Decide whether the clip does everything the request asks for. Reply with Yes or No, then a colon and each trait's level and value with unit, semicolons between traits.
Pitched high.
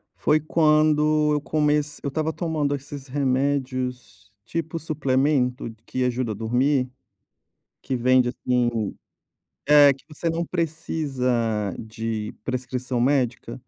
No: low, 135 Hz